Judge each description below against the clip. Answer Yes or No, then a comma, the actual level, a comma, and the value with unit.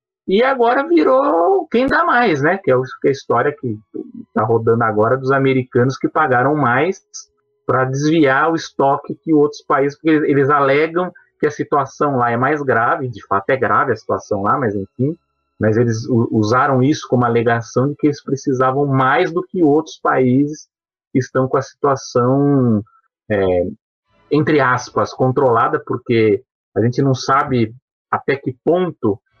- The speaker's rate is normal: Yes, average, 160 wpm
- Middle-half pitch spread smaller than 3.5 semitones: No, average, 4.3 semitones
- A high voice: No, low, 135 Hz